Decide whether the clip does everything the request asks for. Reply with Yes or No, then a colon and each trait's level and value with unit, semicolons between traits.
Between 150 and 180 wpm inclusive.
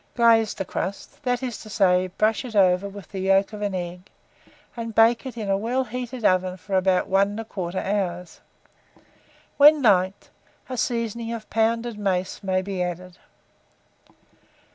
Yes: average, 160 wpm